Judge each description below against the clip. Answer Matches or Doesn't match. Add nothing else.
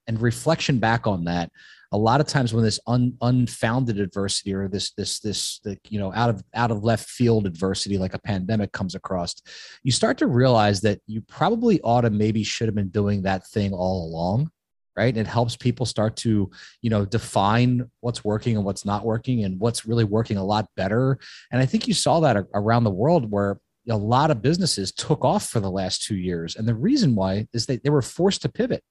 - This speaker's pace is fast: Matches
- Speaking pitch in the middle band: Doesn't match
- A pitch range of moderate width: Matches